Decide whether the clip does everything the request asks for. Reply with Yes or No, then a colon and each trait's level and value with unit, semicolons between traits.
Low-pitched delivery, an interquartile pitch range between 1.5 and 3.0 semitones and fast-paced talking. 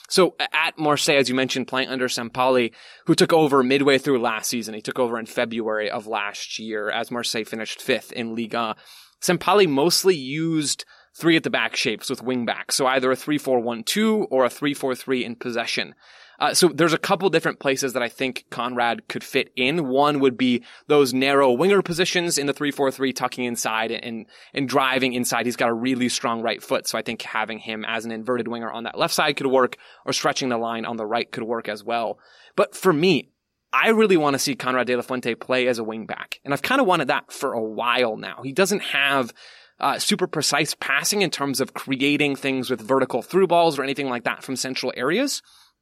No: low, 130 Hz; average, 3.4 semitones; fast, 215 wpm